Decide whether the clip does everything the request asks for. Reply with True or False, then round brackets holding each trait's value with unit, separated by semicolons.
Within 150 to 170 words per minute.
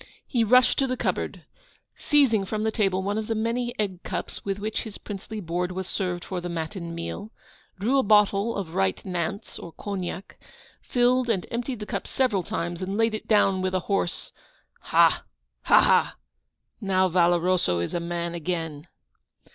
False (180 wpm)